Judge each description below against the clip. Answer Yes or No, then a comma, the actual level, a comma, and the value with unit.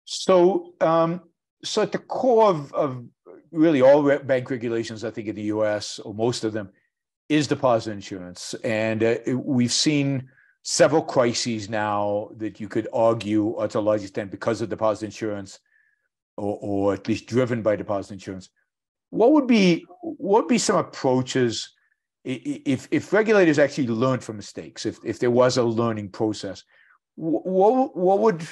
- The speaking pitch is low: Yes, low, 125 Hz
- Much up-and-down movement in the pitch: Yes, wide, 6.9 semitones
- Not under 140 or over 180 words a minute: Yes, average, 165 wpm